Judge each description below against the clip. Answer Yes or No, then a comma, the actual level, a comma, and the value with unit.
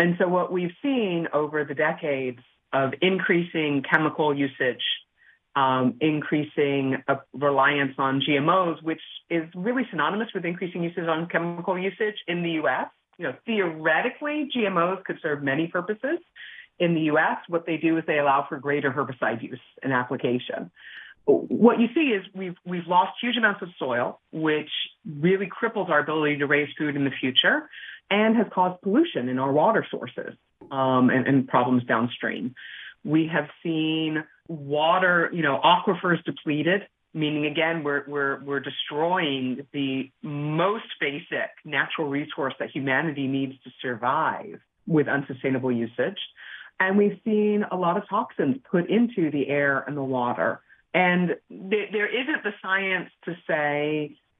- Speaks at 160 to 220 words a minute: No, average, 150 wpm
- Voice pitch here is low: No, medium, 160 Hz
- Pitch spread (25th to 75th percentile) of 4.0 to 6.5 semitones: Yes, average, 4.9 semitones